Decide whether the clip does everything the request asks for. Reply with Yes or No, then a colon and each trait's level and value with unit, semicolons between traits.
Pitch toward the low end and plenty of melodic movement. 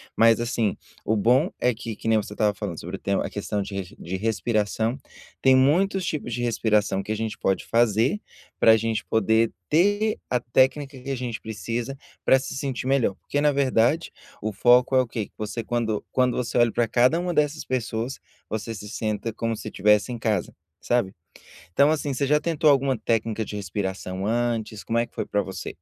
No: low, 115 Hz; average, 3.7 semitones